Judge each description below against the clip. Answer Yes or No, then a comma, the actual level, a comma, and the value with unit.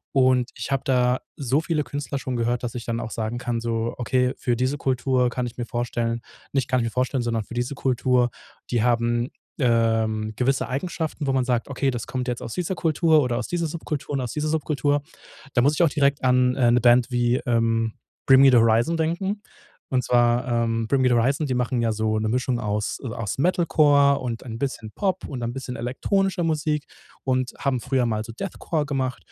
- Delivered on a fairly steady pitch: No, average, 3.0 semitones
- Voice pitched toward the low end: Yes, low, 125 Hz